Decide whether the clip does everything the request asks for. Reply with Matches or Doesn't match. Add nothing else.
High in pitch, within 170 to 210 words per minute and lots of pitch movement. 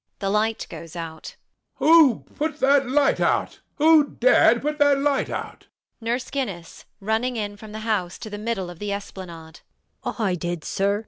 Matches